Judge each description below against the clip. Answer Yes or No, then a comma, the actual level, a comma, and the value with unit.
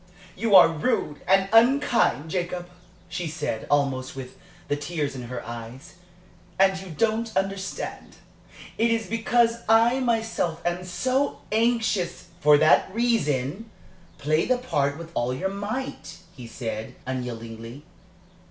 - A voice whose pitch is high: No, medium, 175 Hz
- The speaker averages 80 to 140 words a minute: Yes, slow, 135 wpm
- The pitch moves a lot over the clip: Yes, wide, 8.0 semitones